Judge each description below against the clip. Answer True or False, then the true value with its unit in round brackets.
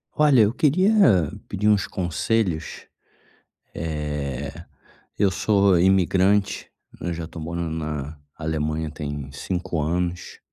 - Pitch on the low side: True (85 Hz)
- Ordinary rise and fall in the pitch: True (4.2 semitones)